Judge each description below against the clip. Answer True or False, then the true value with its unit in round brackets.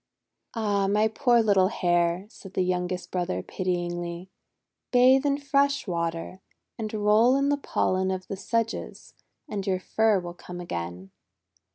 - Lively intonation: False (4.0 semitones)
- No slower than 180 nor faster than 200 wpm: False (145 wpm)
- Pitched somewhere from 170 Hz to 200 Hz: True (190 Hz)